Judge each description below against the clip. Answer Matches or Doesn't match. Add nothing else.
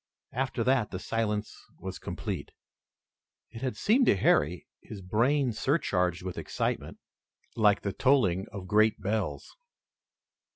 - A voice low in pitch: Matches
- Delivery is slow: Matches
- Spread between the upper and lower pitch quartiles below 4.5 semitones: Doesn't match